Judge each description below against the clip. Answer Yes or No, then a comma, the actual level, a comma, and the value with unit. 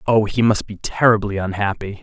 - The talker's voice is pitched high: No, low, 105 Hz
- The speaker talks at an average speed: Yes, average, 180 wpm